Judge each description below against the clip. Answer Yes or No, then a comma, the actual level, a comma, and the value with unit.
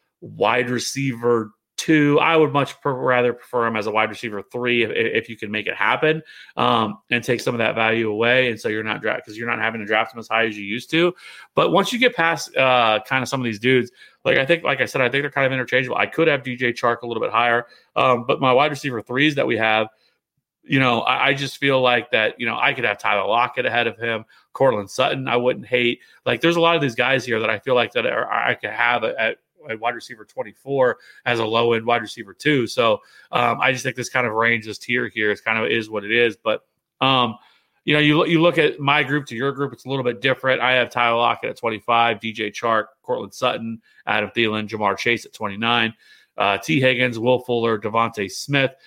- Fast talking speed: Yes, fast, 250 wpm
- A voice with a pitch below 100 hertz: No, low, 120 Hz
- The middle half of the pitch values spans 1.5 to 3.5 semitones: Yes, average, 3.2 semitones